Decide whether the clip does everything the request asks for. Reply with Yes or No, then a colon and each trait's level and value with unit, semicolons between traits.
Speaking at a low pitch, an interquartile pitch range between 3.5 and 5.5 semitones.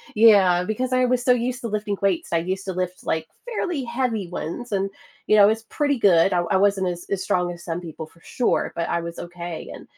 No: high, 195 Hz; average, 5.2 semitones